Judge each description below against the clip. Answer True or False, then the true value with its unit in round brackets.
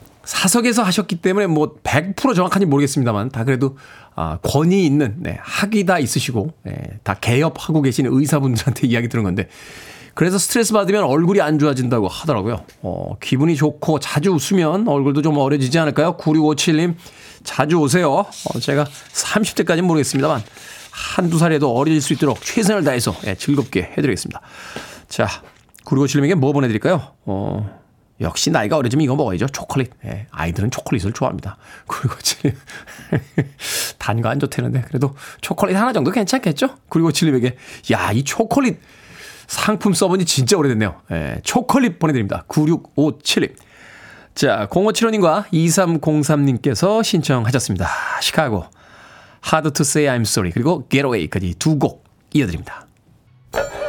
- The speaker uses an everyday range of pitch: False (5.8 semitones)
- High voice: False (145 Hz)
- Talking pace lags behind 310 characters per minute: False (335 characters per minute)